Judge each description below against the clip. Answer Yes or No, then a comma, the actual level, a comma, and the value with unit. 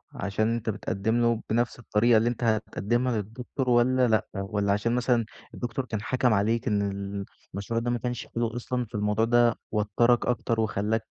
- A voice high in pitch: No, low, 115 Hz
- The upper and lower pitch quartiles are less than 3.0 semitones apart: Yes, narrow, 2.5 semitones